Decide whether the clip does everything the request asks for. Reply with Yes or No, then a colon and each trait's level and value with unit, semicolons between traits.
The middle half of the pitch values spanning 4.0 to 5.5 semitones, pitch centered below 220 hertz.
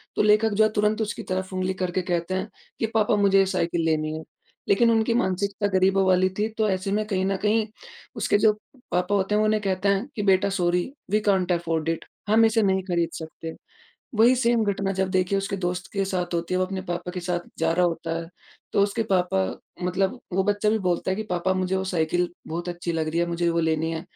No: average, 2.8 semitones; high, 190 Hz